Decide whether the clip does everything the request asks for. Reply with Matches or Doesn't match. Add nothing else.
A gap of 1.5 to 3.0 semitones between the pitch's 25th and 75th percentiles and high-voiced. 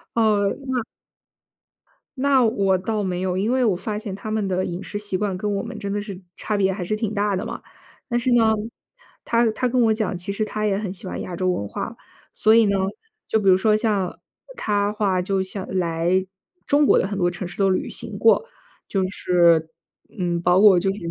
Matches